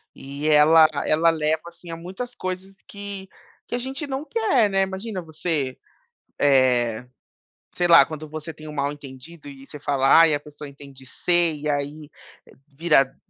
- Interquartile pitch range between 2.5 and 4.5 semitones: Yes, average, 4.2 semitones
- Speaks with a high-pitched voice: No, medium, 155 Hz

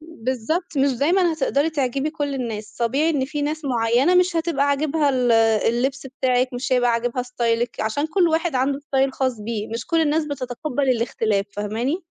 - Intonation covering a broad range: No, average, 4.2 semitones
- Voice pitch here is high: Yes, very high, 270 Hz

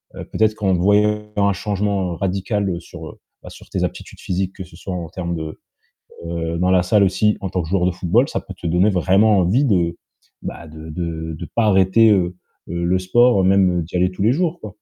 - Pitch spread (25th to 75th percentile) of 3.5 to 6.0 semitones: No, average, 2.9 semitones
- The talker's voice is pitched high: No, very low, 95 Hz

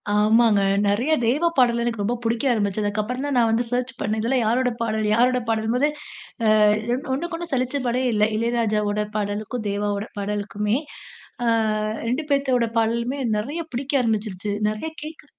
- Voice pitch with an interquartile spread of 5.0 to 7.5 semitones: No, average, 3.1 semitones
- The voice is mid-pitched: No, high, 230 Hz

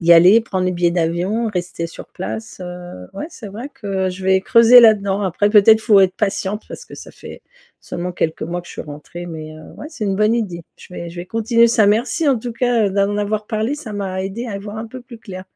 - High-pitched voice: Yes, high, 200 Hz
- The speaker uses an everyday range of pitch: Yes, average, 3.8 semitones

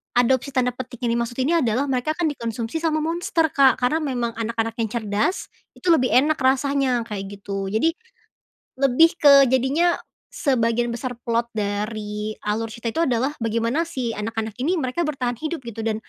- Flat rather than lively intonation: No, average, 3.6 semitones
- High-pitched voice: Yes, high, 245 Hz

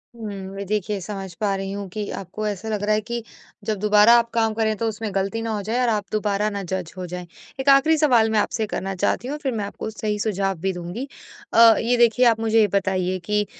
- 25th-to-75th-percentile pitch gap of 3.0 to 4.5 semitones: No, narrow, 2.6 semitones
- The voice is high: Yes, high, 210 Hz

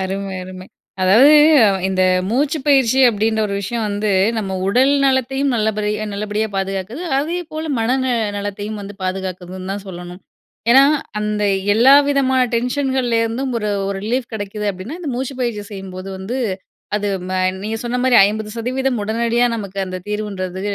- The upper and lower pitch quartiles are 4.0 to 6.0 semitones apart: Yes, average, 4.5 semitones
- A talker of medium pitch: No, high, 215 Hz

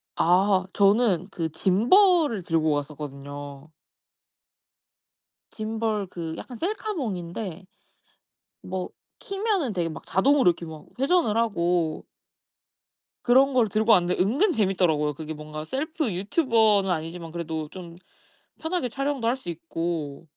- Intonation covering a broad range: Yes, wide, 6.9 semitones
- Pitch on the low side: No, high, 190 Hz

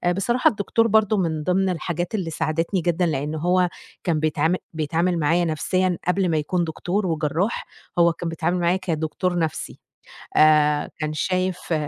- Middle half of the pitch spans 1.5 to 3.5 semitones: Yes, average, 2.7 semitones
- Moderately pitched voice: Yes, medium, 170 Hz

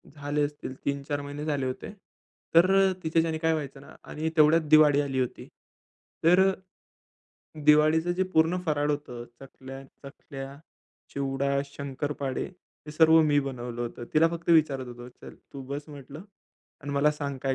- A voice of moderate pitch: Yes, medium, 145 Hz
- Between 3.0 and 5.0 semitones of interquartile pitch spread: No, narrow, 2.4 semitones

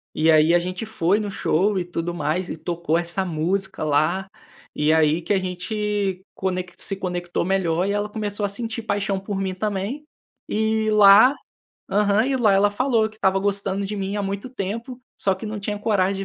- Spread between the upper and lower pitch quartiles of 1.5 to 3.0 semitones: Yes, narrow, 2.6 semitones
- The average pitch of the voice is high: Yes, high, 195 Hz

